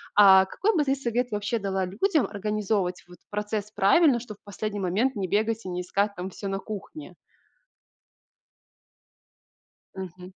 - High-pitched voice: Yes, high, 205 Hz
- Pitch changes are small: No, average, 3.1 semitones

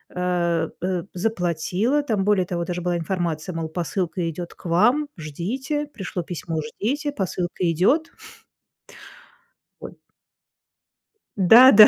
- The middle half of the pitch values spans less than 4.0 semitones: No, average, 4.3 semitones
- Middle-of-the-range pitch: Yes, medium, 180 Hz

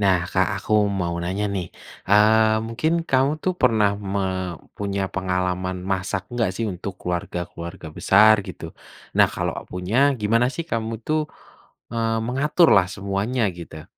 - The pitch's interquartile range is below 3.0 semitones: No, average, 3.9 semitones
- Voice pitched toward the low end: Yes, low, 100 Hz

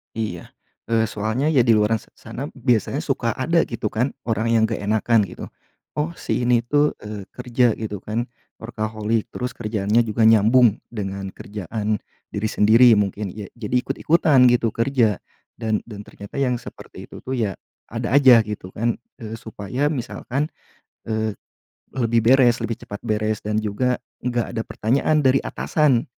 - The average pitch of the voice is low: Yes, low, 115 Hz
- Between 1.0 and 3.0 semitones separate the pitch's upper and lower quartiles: Yes, average, 2.7 semitones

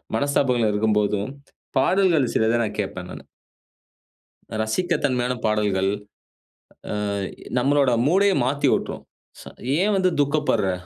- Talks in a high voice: No, low, 125 Hz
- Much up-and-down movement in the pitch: Yes, wide, 5.7 semitones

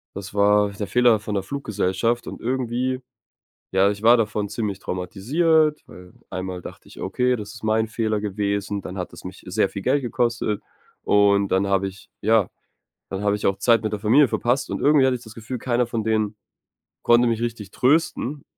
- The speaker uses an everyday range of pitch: Yes, average, 3.4 semitones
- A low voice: Yes, low, 110 Hz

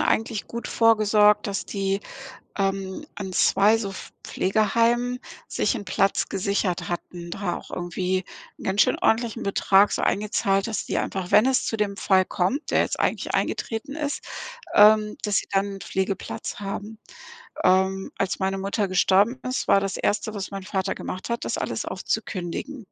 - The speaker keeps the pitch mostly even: Yes, narrow, 2.2 semitones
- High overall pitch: Yes, high, 200 Hz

